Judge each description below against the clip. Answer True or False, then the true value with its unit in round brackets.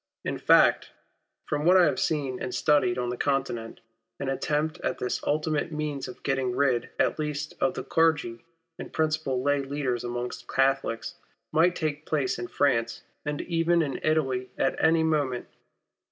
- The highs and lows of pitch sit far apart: False (3.3 semitones)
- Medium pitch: True (145 Hz)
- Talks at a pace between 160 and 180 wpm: True (165 wpm)